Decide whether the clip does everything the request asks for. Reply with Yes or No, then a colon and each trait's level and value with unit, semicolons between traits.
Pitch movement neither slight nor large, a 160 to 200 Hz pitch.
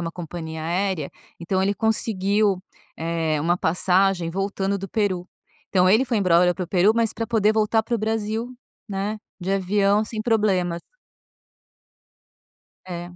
Yes: average, 3.3 semitones; high, 195 Hz